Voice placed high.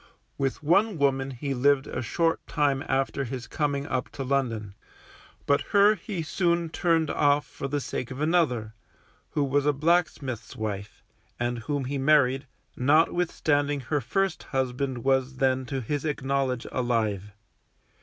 No: medium, 140 Hz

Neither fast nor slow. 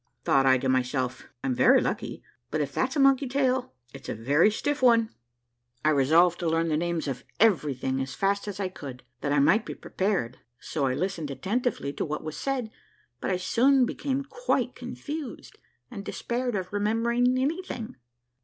Yes: average, 180 wpm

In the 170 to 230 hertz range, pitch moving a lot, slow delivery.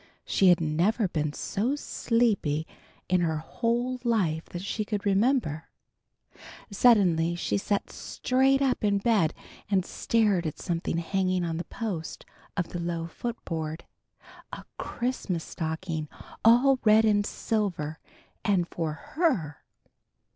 Yes: high, 190 Hz; wide, 5.7 semitones; slow, 125 wpm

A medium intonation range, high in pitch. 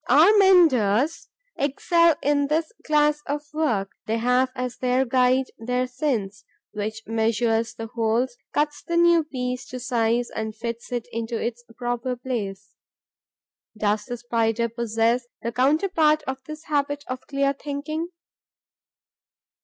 Yes: average, 4.2 semitones; very high, 250 Hz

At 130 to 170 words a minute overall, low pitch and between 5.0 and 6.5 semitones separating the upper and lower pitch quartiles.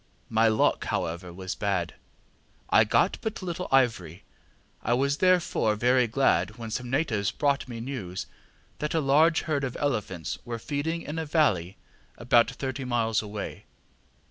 Yes: average, 150 wpm; low, 120 Hz; wide, 5.4 semitones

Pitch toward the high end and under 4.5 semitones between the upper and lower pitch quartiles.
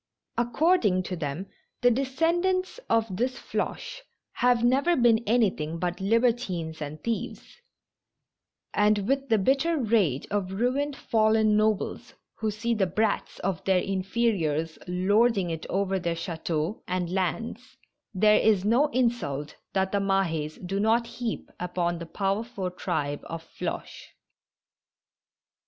No: high, 210 Hz; average, 4.8 semitones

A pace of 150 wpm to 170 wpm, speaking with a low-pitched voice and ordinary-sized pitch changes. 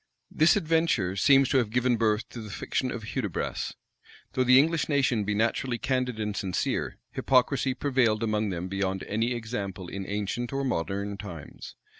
Yes: average, 165 wpm; low, 115 Hz; average, 4.3 semitones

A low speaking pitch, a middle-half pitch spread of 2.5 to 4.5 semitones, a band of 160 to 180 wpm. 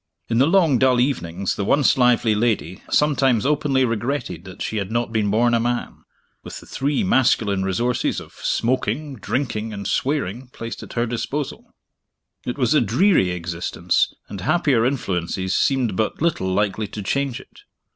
No: low, 120 Hz; average, 5.0 semitones; average, 165 wpm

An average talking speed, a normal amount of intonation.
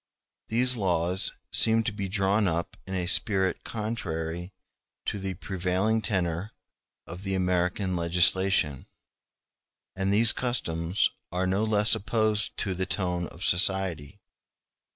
No: slow, 125 wpm; average, 3.1 semitones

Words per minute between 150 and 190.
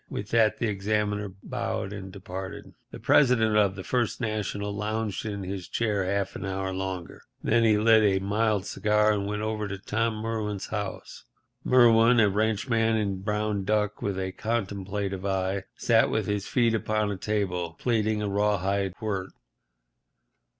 Yes: average, 165 wpm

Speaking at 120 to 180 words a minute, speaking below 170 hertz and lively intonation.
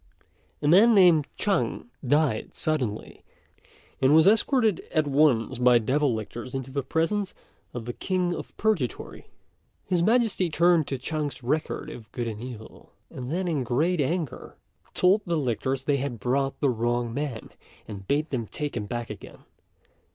Yes: average, 160 wpm; medium, 140 Hz; wide, 5.7 semitones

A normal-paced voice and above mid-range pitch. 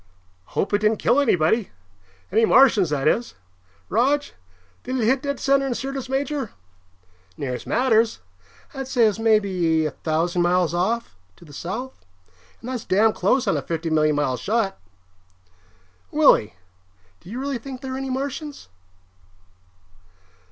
Yes: average, 150 wpm; high, 225 Hz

